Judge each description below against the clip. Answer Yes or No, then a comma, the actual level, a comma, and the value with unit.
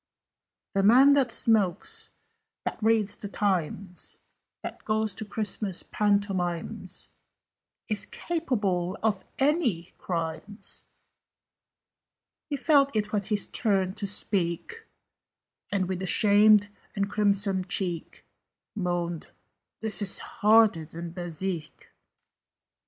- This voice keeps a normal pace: No, slow, 100 wpm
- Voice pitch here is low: No, high, 200 Hz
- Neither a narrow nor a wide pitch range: Yes, average, 3.2 semitones